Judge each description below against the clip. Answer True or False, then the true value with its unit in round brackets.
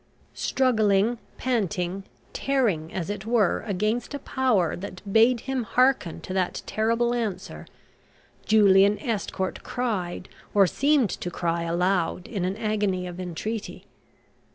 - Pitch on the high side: True (205 Hz)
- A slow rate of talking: True (125 wpm)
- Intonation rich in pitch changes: False (4.5 semitones)